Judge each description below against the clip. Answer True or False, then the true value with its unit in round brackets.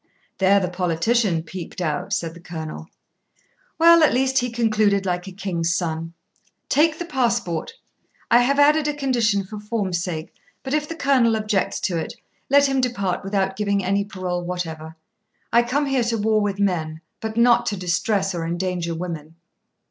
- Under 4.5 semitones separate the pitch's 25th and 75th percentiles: False (5.3 semitones)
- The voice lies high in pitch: True (200 Hz)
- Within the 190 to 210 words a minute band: False (175 wpm)